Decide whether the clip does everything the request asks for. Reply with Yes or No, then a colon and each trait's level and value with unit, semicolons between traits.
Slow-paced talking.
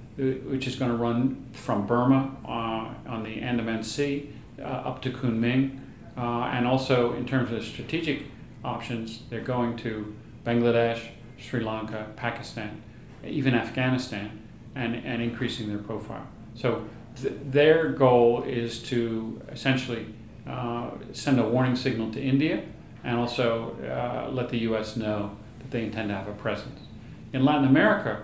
No: average, 145 wpm